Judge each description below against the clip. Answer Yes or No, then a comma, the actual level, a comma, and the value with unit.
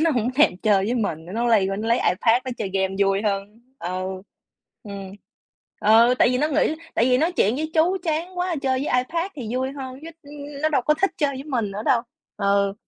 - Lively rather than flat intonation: Yes, wide, 6.5 semitones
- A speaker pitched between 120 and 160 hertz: No, high, 245 Hz